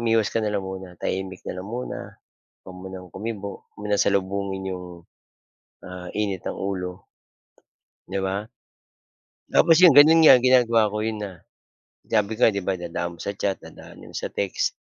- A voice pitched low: Yes, low, 100 Hz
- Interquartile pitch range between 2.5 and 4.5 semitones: Yes, average, 2.9 semitones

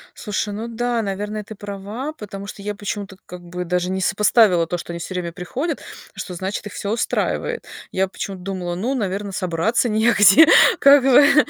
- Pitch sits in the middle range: No, high, 205 Hz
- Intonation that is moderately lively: Yes, average, 3.5 semitones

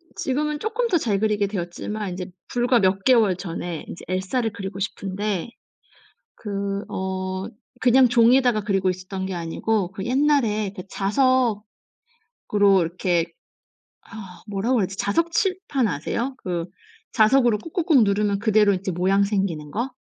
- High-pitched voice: Yes, high, 205 Hz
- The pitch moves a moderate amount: Yes, average, 4.5 semitones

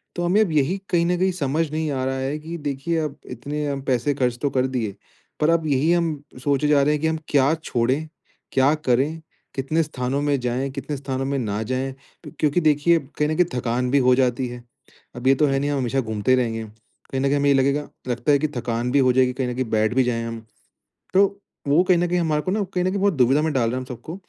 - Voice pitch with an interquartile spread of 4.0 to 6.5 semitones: No, average, 3.5 semitones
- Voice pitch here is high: No, medium, 140 Hz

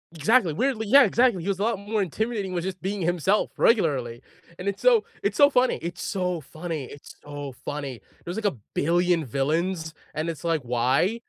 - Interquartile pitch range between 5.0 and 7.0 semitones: Yes, wide, 5.5 semitones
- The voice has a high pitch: No, medium, 175 Hz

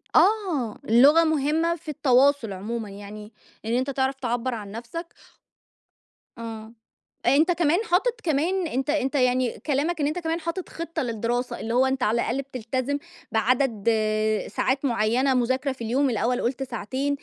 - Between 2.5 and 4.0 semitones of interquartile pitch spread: No, average, 4.4 semitones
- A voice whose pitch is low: No, very high, 265 Hz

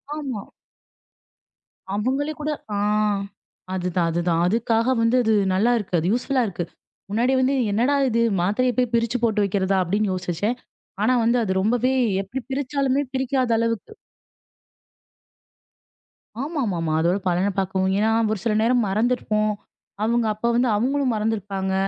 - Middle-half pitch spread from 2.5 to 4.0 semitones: No, average, 4.5 semitones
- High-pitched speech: Yes, high, 225 Hz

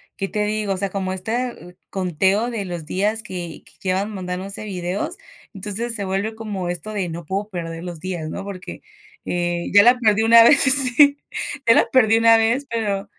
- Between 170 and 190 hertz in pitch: No, high, 200 Hz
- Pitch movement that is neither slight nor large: Yes, average, 3.6 semitones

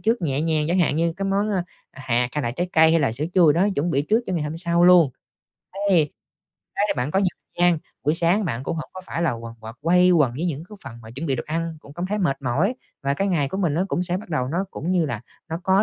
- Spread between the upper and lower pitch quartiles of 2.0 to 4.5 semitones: Yes, average, 4.2 semitones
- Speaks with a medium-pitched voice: Yes, medium, 165 Hz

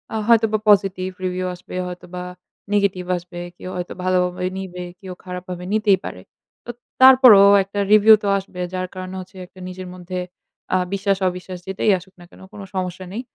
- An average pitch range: No, narrow, 1.7 semitones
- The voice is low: No, medium, 185 Hz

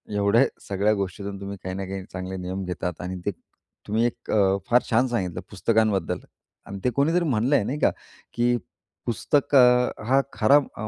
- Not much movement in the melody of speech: No, average, 4.2 semitones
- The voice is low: Yes, low, 105 Hz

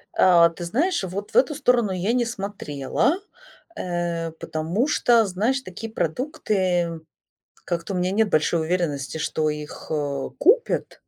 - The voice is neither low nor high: Yes, medium, 180 Hz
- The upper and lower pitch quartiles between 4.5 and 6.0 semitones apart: Yes, wide, 5.5 semitones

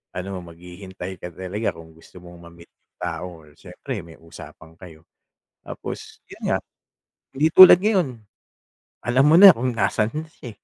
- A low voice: Yes, very low, 95 Hz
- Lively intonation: Yes, wide, 7.0 semitones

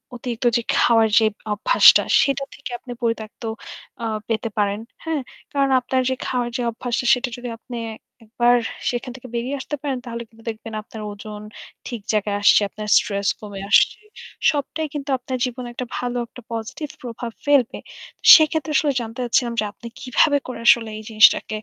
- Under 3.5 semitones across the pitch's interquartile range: Yes, average, 2.7 semitones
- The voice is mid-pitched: No, high, 240 Hz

